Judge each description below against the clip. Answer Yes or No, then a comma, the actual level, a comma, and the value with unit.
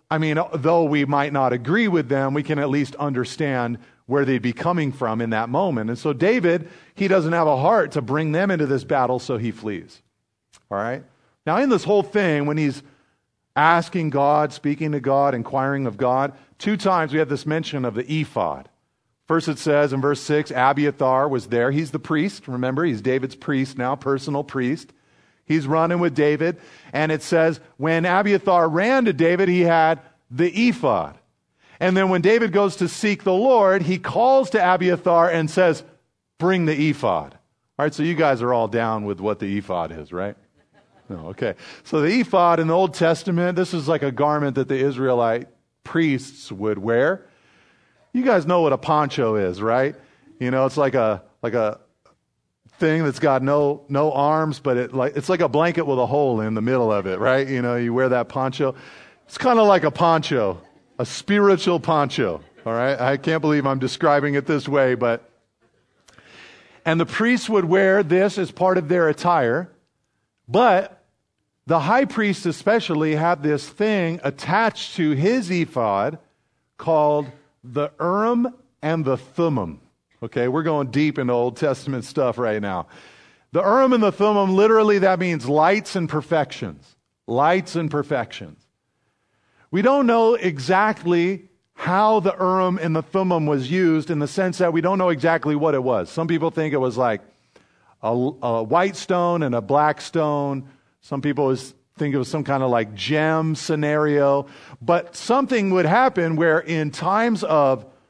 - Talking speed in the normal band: Yes, average, 180 wpm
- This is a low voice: No, medium, 150 Hz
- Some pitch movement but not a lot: Yes, average, 4.9 semitones